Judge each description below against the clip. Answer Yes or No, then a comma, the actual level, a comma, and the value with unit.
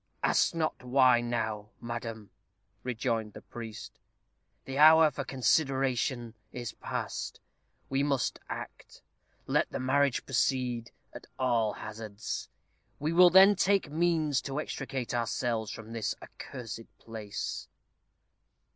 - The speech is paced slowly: Yes, slow, 115 wpm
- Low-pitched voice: Yes, low, 125 Hz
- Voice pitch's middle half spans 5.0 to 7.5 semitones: No, average, 3.7 semitones